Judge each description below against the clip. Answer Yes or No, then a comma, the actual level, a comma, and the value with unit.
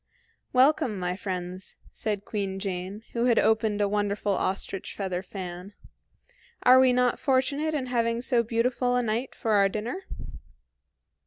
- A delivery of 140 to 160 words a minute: Yes, average, 145 wpm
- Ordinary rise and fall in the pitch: Yes, average, 4.2 semitones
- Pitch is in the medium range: No, high, 215 Hz